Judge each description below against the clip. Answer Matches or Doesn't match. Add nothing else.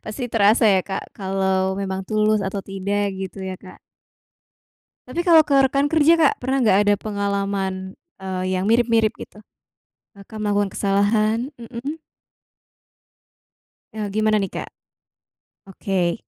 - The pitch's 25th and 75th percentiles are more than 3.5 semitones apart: Doesn't match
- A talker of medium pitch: Doesn't match